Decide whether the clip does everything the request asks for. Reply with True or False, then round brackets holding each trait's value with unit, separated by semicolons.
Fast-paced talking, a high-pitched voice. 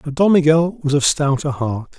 False (210 wpm; 145 Hz)